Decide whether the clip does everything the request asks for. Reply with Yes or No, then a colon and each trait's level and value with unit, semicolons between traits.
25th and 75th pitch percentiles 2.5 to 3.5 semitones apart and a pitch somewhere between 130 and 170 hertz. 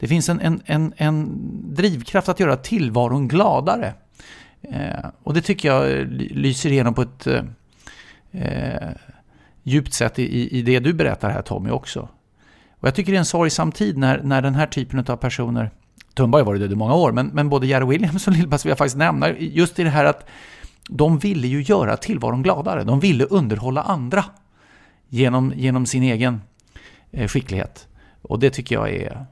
No: average, 4.8 semitones; medium, 140 Hz